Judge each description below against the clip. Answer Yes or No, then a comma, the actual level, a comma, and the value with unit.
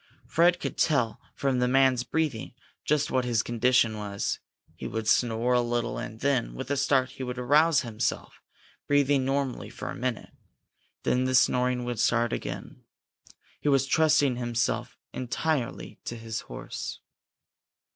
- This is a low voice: Yes, low, 125 Hz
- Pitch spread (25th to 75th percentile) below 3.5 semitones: Yes, narrow, 2.6 semitones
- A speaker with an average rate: Yes, average, 150 wpm